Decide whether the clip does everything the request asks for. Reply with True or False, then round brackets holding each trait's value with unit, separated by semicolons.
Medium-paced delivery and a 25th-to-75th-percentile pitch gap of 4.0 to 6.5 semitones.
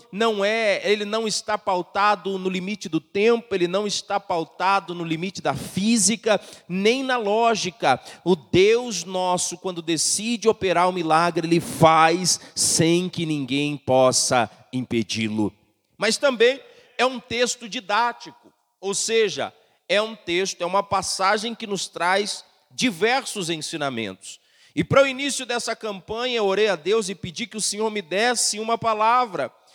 True (150 wpm; 4.7 semitones)